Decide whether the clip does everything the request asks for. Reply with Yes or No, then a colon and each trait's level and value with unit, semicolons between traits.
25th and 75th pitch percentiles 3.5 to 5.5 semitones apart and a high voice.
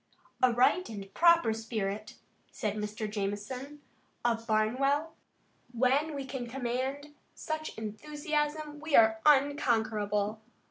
Yes: average, 5.2 semitones; high, 245 Hz